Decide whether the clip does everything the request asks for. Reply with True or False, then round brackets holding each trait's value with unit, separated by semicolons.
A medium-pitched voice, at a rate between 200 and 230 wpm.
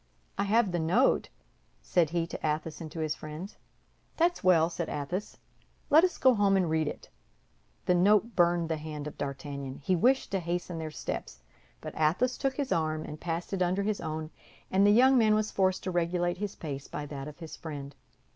True (175 Hz; 205 wpm)